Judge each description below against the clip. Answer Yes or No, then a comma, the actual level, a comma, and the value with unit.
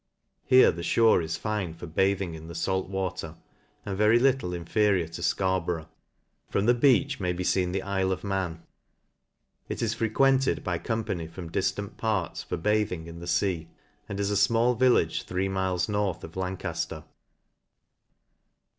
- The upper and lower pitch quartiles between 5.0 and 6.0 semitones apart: No, average, 3.5 semitones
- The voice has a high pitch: No, very low, 95 Hz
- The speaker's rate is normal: Yes, average, 160 wpm